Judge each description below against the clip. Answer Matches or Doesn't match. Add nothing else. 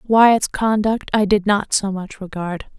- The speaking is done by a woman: Matches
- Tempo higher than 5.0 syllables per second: Doesn't match